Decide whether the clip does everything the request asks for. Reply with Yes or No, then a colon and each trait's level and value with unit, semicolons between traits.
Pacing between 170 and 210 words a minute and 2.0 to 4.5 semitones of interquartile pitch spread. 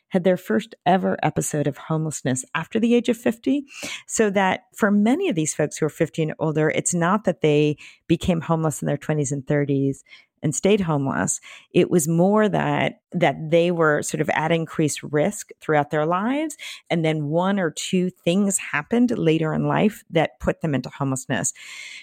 No: average, 185 wpm; average, 5.1 semitones